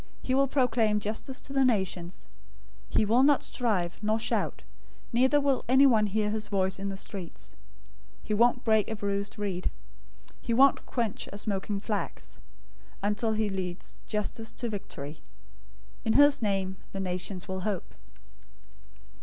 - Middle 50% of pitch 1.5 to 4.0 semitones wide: Yes, average, 3.5 semitones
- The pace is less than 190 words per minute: Yes, average, 155 wpm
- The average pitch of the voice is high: Yes, high, 210 Hz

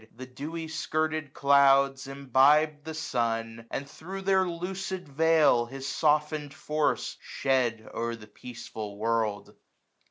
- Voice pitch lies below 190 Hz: Yes, medium, 140 Hz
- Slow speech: Yes, slow, 125 wpm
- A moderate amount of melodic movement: Yes, average, 4.8 semitones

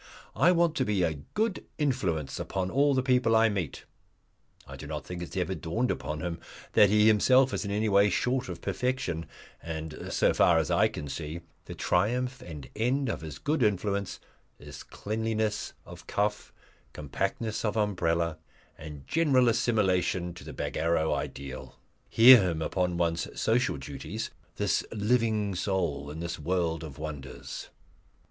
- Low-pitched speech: Yes, very low, 95 Hz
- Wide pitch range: Yes, wide, 5.8 semitones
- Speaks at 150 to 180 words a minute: Yes, average, 160 wpm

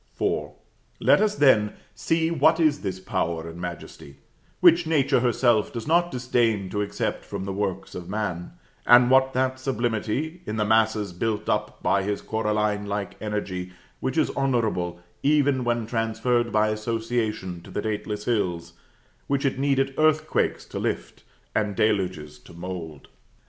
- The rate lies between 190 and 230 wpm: No, average, 155 wpm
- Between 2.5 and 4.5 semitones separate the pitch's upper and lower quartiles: No, average, 5.1 semitones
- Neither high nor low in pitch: No, low, 110 Hz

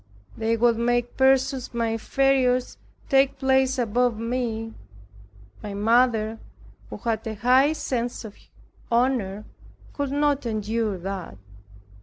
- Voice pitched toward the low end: No, high, 235 Hz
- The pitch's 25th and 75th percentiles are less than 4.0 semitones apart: Yes, average, 3.0 semitones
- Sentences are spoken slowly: Yes, slow, 115 wpm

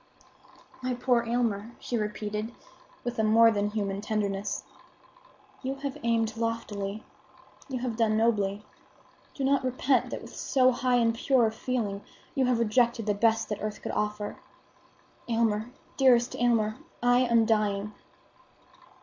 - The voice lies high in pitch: Yes, high, 230 Hz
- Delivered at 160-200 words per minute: No, average, 140 wpm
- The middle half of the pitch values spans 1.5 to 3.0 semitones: Yes, narrow, 2.5 semitones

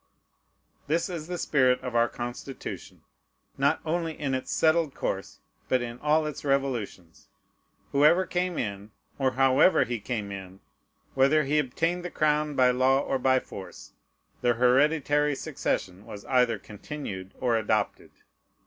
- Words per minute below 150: Yes, average, 140 wpm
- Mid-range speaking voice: No, low, 130 Hz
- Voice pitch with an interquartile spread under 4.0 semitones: No, average, 4.3 semitones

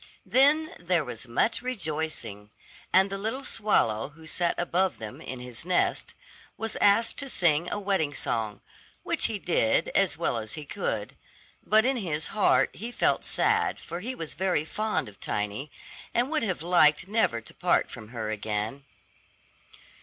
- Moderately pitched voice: Yes, medium, 170 Hz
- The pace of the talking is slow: No, average, 165 wpm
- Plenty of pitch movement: Yes, wide, 9.0 semitones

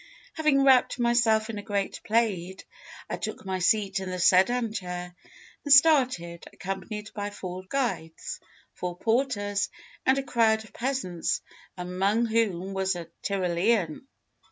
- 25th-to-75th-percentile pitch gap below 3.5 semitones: No, average, 4.4 semitones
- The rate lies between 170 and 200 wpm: No, slow, 135 wpm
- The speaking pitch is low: No, high, 205 Hz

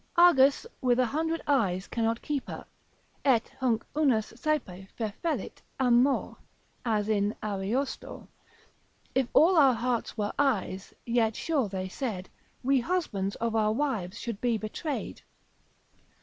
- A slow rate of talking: Yes, slow, 130 wpm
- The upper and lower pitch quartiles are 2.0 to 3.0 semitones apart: No, average, 4.6 semitones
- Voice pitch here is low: No, high, 235 Hz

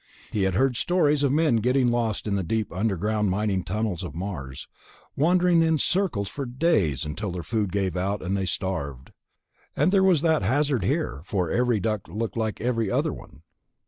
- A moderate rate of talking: Yes, average, 185 wpm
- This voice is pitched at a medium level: No, low, 110 Hz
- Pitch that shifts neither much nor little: No, wide, 6.3 semitones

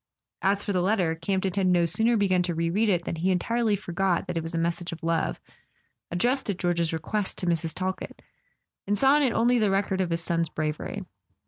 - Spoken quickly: Yes, fast, 225 wpm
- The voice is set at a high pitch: No, medium, 180 Hz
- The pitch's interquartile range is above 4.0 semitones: No, average, 3.3 semitones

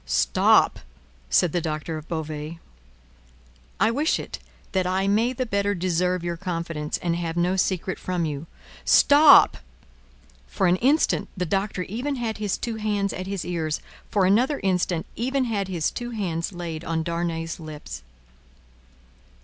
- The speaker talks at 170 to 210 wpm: No, average, 150 wpm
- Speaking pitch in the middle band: Yes, medium, 180 Hz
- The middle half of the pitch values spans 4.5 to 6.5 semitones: No, average, 4.0 semitones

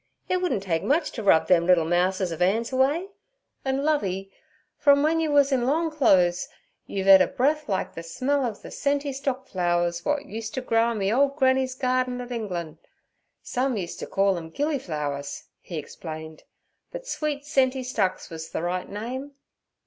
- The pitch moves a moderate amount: No, wide, 7.5 semitones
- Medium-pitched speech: No, high, 235 Hz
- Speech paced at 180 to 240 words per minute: Yes, average, 185 wpm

